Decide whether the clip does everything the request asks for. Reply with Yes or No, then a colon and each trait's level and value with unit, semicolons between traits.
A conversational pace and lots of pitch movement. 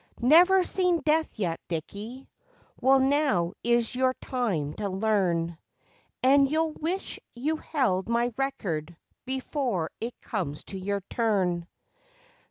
No: slow, 120 wpm; wide, 6.9 semitones